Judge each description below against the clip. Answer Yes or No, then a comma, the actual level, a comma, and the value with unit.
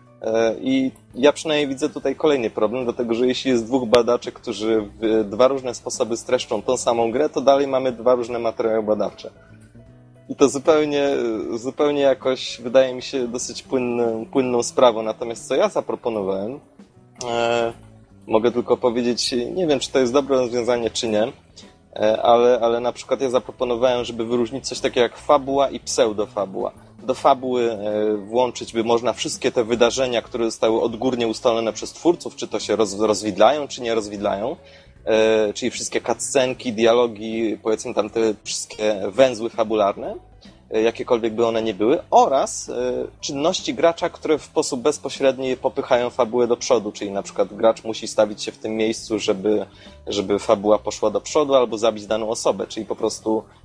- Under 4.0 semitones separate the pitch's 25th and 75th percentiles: Yes, average, 2.9 semitones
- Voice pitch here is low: Yes, low, 120 Hz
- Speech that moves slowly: No, fast, 160 wpm